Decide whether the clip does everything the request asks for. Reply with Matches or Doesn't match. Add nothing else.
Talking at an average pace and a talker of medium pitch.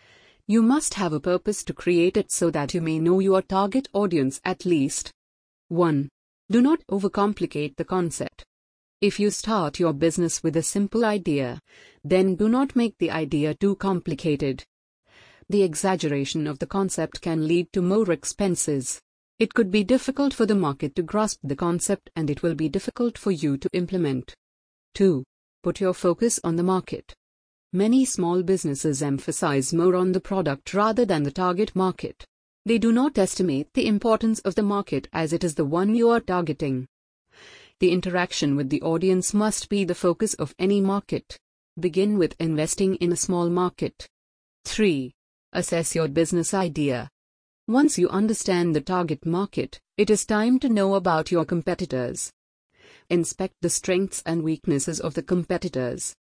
Matches